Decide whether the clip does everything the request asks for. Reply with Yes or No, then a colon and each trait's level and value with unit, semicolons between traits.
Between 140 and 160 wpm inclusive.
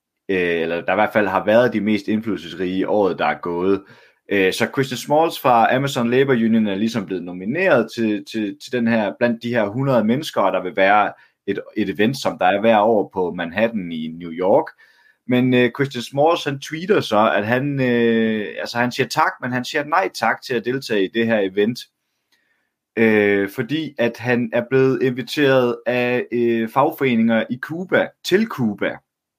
No: average, 180 wpm